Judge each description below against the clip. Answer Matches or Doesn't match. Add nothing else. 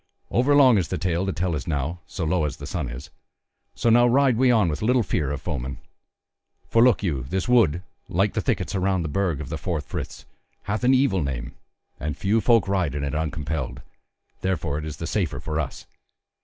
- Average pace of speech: Doesn't match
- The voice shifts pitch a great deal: Matches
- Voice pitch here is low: Matches